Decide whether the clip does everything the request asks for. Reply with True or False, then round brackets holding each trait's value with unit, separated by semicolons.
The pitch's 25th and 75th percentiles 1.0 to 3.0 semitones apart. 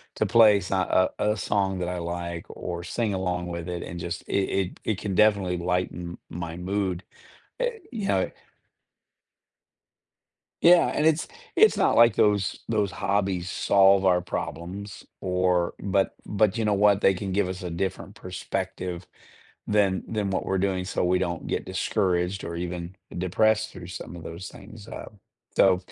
True (2.4 semitones)